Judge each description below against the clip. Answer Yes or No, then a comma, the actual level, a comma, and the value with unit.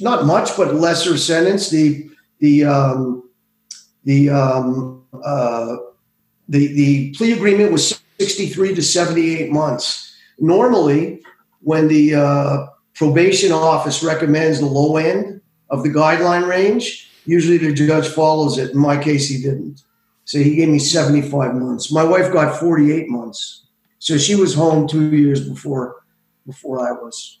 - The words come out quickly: No, average, 140 wpm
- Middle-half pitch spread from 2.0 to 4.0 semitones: Yes, average, 3.1 semitones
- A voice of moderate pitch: Yes, medium, 155 Hz